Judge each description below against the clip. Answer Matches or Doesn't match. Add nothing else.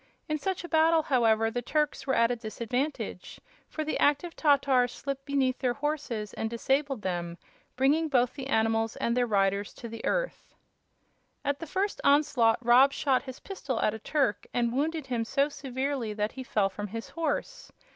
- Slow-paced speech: Doesn't match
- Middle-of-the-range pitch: Doesn't match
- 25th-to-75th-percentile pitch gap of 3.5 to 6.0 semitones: Matches